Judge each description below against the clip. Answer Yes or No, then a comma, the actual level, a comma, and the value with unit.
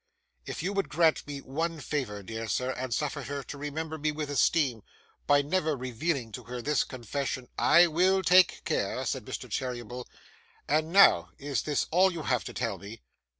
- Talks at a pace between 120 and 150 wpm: No, average, 190 wpm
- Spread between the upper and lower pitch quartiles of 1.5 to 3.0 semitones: No, average, 4.3 semitones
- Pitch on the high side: No, medium, 145 Hz